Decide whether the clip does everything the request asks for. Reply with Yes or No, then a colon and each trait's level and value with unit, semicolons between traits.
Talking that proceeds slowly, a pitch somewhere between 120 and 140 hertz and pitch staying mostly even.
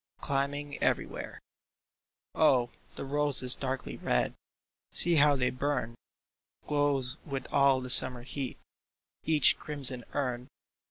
Yes: slow, 115 wpm; low, 135 Hz; narrow, 2.3 semitones